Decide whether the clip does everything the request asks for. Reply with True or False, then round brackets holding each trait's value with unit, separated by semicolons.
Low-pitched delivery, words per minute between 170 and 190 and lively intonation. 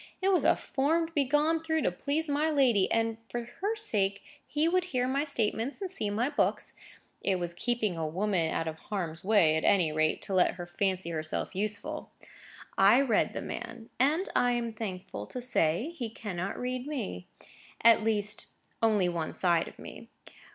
False (220 Hz; 185 wpm; 7.5 semitones)